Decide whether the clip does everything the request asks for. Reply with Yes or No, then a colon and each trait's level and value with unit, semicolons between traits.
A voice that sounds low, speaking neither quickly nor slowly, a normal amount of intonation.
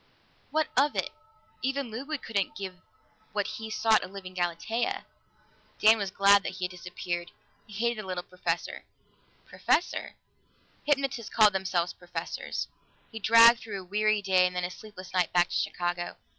No: high, 200 Hz; average, 160 wpm; average, 3.8 semitones